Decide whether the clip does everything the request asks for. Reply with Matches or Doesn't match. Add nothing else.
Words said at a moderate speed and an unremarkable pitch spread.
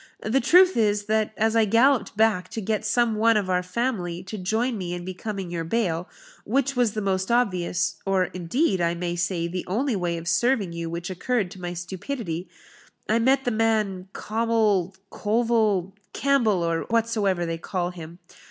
Matches